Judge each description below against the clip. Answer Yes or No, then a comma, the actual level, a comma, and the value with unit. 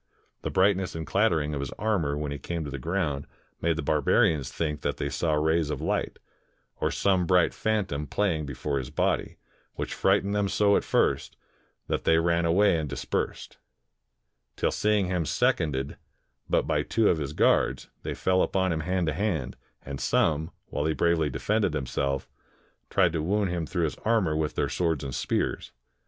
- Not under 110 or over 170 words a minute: No, average, 180 wpm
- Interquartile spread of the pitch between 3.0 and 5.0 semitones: Yes, average, 4.2 semitones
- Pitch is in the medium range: No, very low, 80 Hz